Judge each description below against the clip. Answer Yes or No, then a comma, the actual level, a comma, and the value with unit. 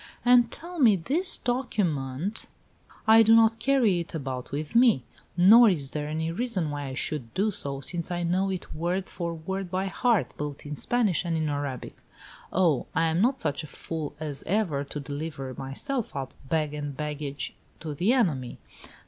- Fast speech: No, average, 180 wpm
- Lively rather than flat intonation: Yes, wide, 6.7 semitones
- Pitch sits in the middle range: Yes, medium, 170 Hz